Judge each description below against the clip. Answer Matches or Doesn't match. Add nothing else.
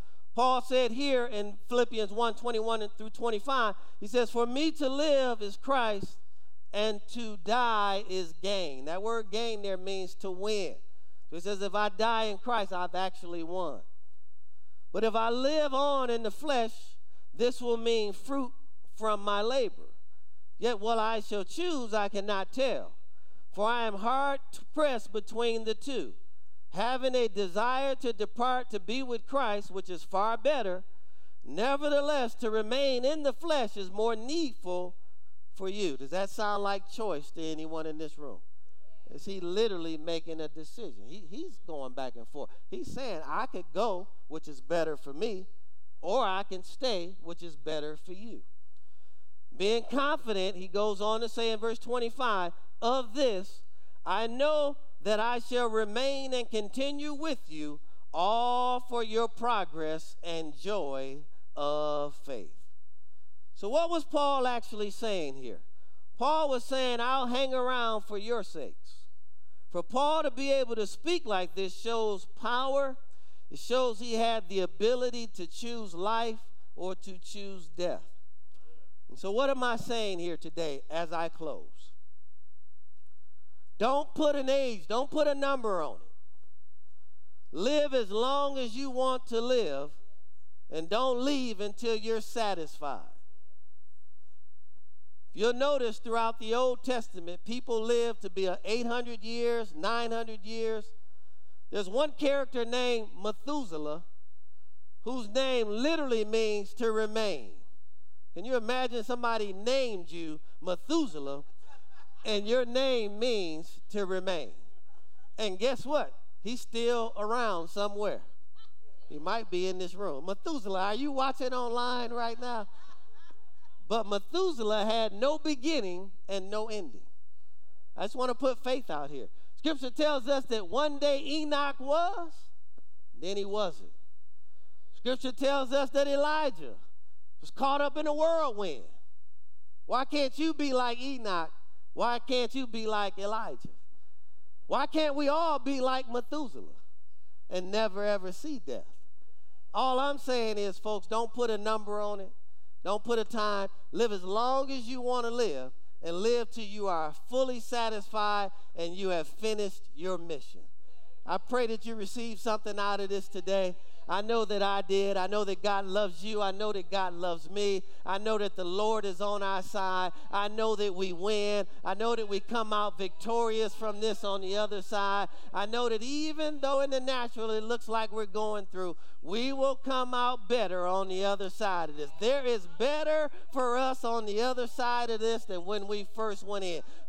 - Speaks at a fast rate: Doesn't match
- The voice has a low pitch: Doesn't match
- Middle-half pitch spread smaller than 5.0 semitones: Doesn't match